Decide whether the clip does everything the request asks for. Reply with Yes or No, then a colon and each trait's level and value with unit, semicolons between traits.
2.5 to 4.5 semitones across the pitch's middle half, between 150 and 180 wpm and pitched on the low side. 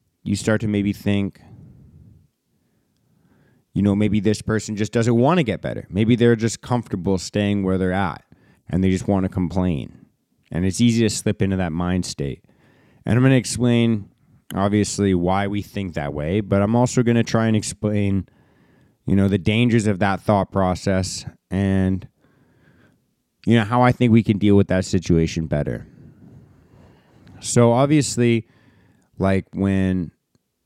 Yes: average, 3.4 semitones; average, 160 wpm; low, 100 Hz